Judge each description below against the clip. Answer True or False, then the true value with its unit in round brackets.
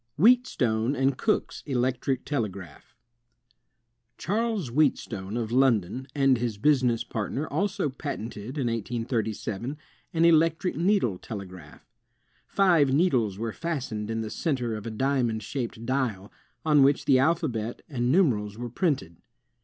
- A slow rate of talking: True (130 wpm)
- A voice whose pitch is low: True (125 Hz)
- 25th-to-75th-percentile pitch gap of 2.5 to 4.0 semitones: False (5.2 semitones)